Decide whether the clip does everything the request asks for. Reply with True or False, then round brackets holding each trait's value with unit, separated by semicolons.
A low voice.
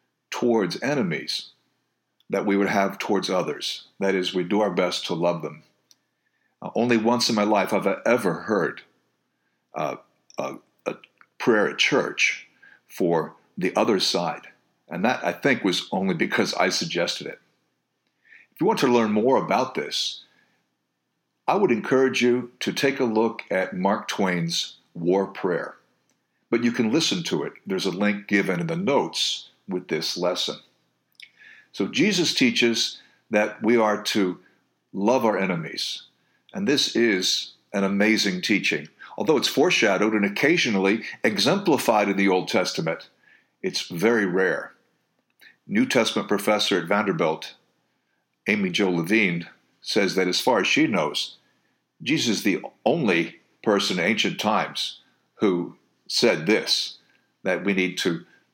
True (105 Hz)